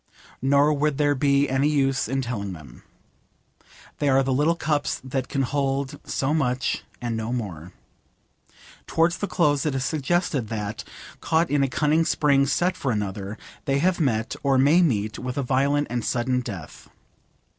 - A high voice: No, low, 135 Hz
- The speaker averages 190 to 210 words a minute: No, average, 165 wpm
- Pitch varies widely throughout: No, average, 3.2 semitones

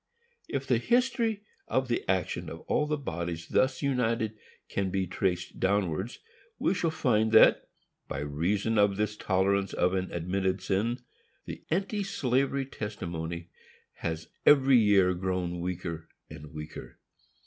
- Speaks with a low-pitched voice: Yes, low, 100 Hz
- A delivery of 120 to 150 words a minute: Yes, slow, 135 wpm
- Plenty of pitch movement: Yes, wide, 6.5 semitones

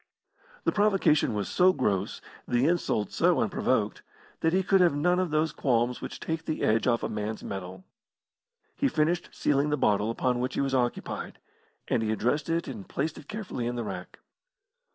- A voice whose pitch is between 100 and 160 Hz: Yes, medium, 140 Hz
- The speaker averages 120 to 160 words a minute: No, average, 185 wpm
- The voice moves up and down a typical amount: No, wide, 6.7 semitones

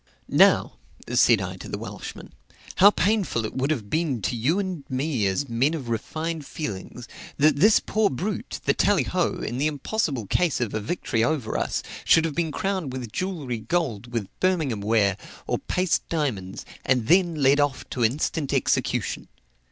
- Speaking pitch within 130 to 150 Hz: Yes, medium, 140 Hz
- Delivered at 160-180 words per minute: Yes, average, 170 wpm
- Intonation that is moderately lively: No, wide, 6.1 semitones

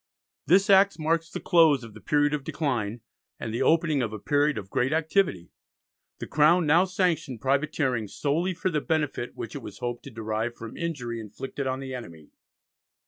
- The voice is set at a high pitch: No, medium, 140 Hz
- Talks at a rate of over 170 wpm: Yes, average, 185 wpm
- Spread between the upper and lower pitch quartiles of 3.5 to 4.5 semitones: No, wide, 5.5 semitones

